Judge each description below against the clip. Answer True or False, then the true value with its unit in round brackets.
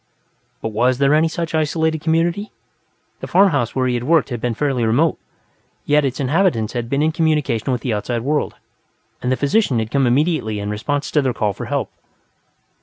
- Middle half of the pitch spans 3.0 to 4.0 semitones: False (4.8 semitones)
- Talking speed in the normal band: True (190 wpm)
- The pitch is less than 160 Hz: True (140 Hz)